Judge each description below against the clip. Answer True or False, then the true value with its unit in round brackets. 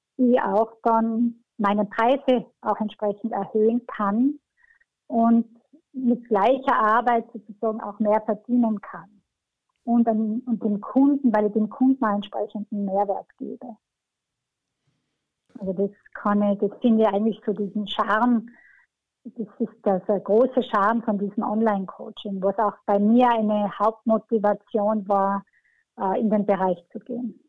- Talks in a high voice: True (220 Hz)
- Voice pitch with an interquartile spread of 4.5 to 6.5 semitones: False (2.5 semitones)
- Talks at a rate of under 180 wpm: True (135 wpm)